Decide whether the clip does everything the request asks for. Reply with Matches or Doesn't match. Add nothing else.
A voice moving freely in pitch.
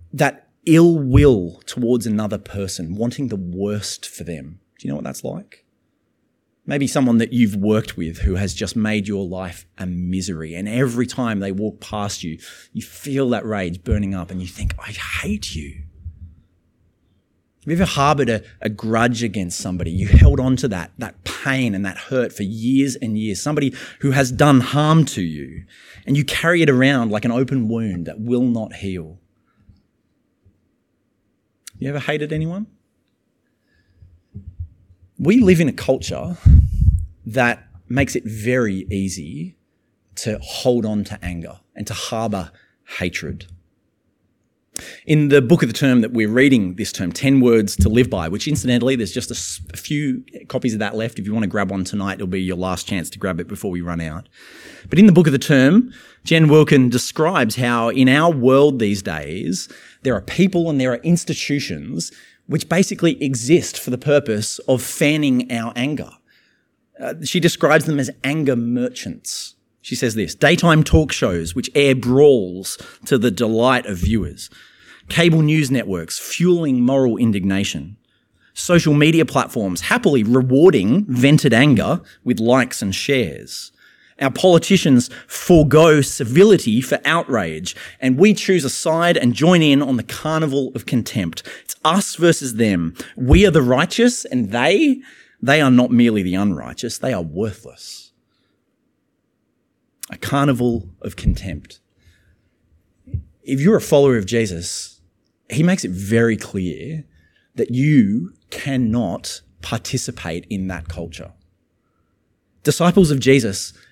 Matches